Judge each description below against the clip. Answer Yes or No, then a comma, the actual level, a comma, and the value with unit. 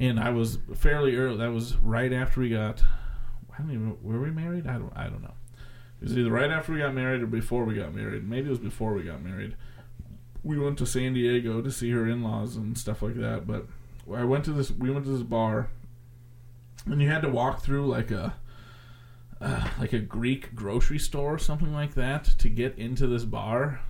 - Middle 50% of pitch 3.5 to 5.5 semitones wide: No, narrow, 2.5 semitones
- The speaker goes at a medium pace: No, fast, 220 wpm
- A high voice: No, low, 120 Hz